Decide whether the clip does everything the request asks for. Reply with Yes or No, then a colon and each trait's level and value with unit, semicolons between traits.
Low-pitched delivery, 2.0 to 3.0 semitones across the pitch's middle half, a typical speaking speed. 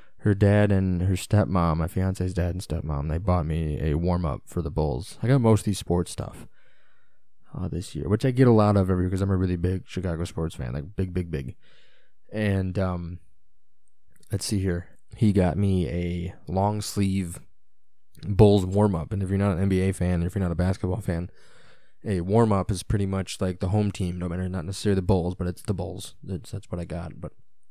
No: very low, 95 Hz; narrow, 2.6 semitones; fast, 215 wpm